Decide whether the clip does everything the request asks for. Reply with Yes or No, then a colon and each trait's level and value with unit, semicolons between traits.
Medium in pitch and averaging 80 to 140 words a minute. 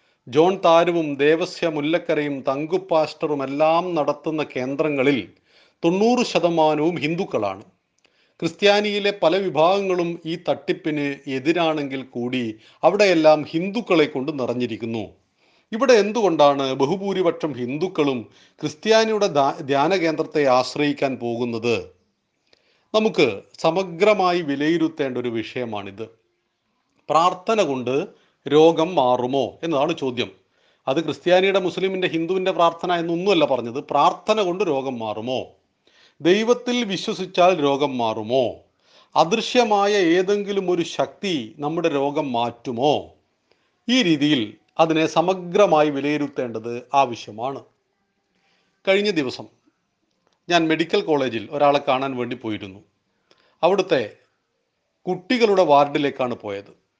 Yes: medium, 155 Hz; average, 85 wpm